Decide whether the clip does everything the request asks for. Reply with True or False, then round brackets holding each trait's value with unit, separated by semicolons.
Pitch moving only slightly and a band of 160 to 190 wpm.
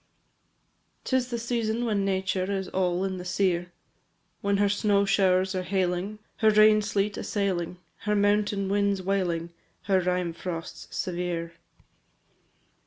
False (2.2 semitones; 135 wpm)